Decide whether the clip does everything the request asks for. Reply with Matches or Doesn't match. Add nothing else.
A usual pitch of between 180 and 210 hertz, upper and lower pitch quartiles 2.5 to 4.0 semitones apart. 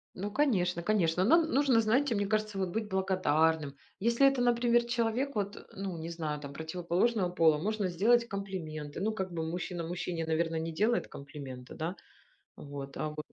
Doesn't match